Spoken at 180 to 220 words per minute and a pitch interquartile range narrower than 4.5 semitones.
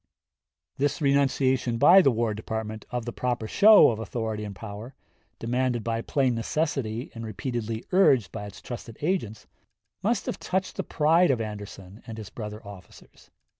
No: average, 160 wpm; average, 4.0 semitones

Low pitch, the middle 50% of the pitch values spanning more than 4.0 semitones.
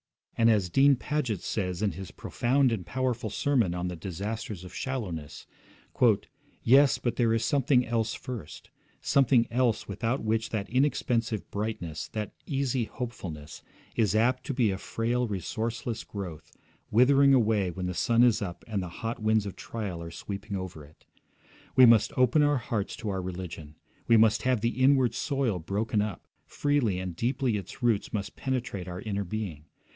Yes: low, 110 Hz; average, 4.5 semitones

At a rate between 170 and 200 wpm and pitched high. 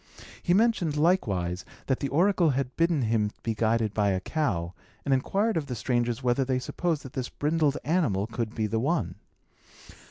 No: average, 180 wpm; low, 130 Hz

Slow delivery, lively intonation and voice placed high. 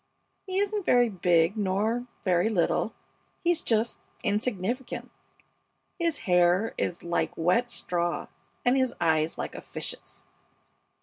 Yes: slow, 120 wpm; wide, 5.8 semitones; high, 210 Hz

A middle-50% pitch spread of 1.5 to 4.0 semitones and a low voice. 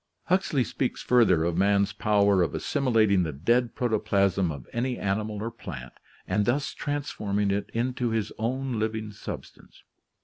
Yes: average, 3.7 semitones; low, 110 Hz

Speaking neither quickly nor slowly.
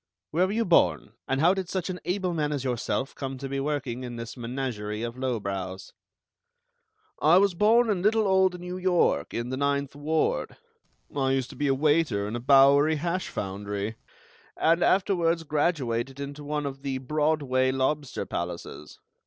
Yes: average, 170 wpm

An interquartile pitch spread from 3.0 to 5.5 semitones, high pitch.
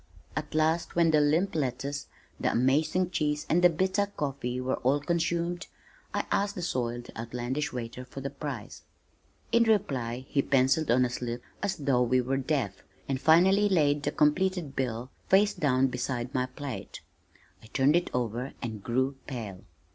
No: average, 4.7 semitones; medium, 140 Hz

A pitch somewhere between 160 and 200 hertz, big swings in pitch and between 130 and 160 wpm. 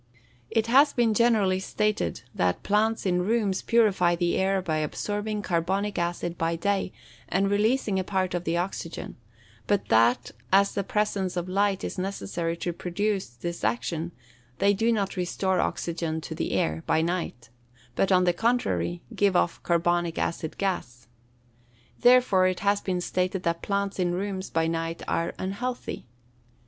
No: medium, 185 Hz; average, 2.9 semitones; average, 155 wpm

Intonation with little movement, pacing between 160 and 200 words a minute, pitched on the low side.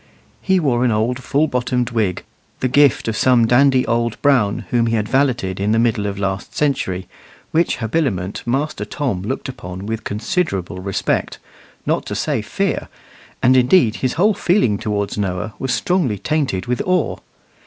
No: average, 5.0 semitones; average, 165 wpm; low, 120 Hz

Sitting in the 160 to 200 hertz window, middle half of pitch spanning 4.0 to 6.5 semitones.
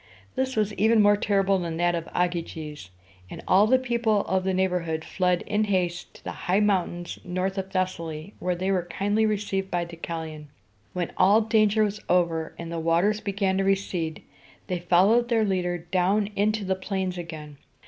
No: medium, 185 Hz; average, 3.0 semitones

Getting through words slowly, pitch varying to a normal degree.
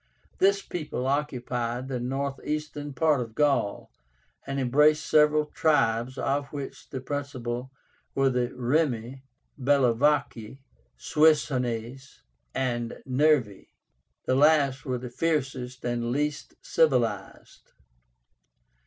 Yes: slow, 100 wpm; average, 3.3 semitones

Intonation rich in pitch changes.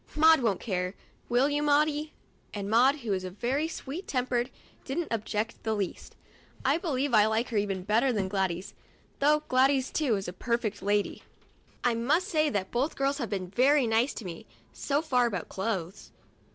Yes: wide, 5.7 semitones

